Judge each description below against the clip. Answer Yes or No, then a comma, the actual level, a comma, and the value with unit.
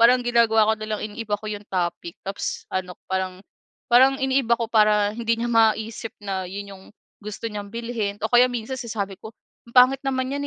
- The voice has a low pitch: No, high, 220 Hz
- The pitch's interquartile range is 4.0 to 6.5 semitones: No, average, 2.8 semitones